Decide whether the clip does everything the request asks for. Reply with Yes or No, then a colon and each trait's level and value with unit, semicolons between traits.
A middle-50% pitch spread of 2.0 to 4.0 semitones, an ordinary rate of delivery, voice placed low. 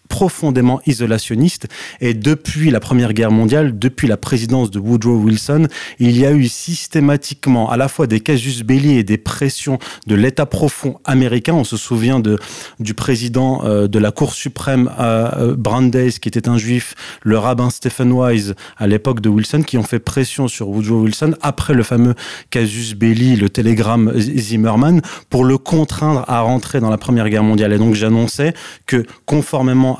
Yes: average, 3.3 semitones; average, 170 wpm; low, 125 Hz